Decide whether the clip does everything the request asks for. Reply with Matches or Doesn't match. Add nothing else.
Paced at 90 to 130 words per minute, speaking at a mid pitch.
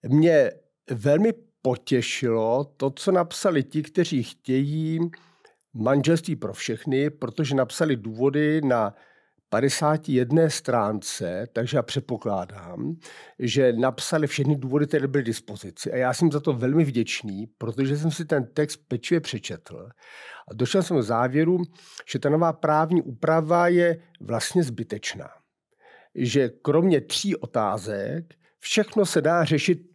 Matches